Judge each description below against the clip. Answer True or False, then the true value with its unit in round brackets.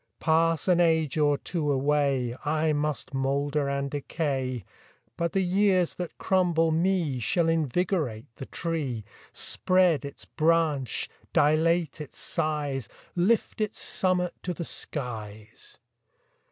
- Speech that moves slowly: True (120 wpm)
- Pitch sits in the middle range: True (155 Hz)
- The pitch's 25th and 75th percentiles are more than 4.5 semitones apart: False (3.8 semitones)